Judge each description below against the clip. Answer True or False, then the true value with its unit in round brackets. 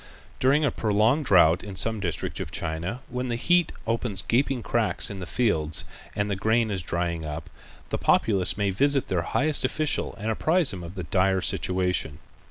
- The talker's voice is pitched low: True (100 Hz)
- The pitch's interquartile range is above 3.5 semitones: True (5.5 semitones)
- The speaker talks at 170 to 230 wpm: True (180 wpm)